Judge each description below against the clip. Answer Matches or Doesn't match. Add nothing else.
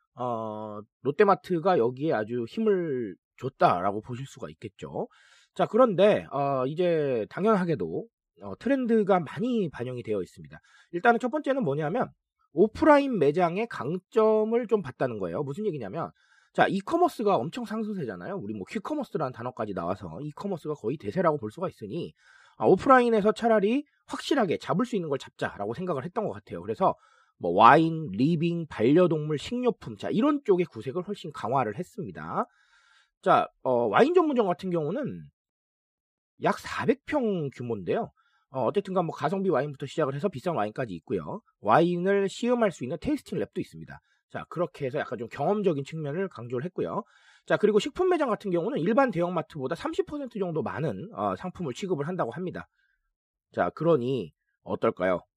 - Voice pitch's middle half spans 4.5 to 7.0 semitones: Doesn't match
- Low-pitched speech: Doesn't match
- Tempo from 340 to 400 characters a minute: Matches